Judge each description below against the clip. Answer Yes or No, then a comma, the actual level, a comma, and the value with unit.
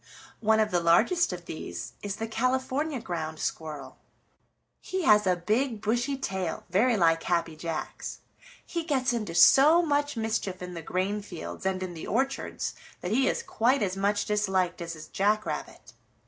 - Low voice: No, high, 205 Hz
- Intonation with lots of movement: Yes, wide, 6.3 semitones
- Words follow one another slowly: No, average, 170 wpm